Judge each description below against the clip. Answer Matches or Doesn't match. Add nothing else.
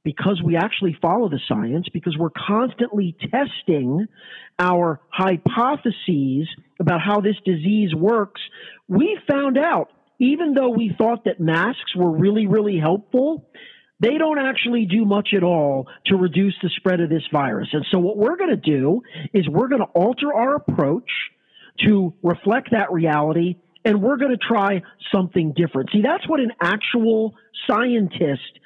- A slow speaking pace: Doesn't match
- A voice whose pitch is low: Doesn't match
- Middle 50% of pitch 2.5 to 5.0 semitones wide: Doesn't match